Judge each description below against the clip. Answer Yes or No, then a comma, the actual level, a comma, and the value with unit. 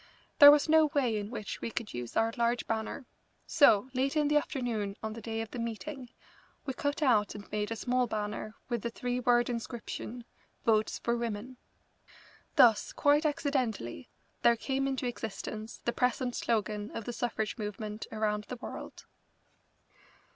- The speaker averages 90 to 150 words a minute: No, average, 165 wpm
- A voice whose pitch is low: No, high, 235 Hz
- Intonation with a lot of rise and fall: No, average, 3.0 semitones